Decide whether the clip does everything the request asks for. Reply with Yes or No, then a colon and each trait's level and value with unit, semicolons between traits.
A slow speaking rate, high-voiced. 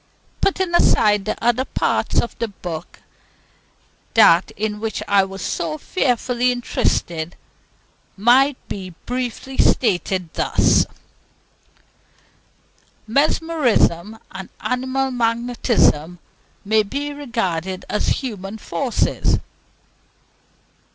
Yes: slow, 90 wpm; high, 225 Hz